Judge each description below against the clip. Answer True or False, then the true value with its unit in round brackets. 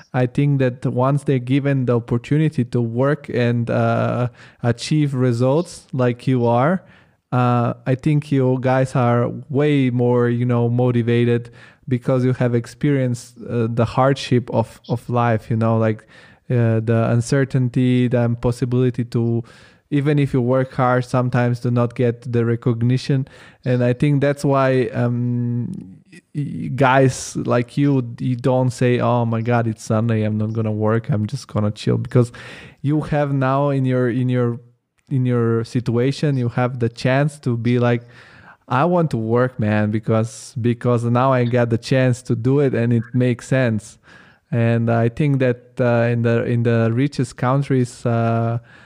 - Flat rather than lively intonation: True (1.8 semitones)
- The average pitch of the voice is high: False (125 Hz)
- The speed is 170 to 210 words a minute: False (160 wpm)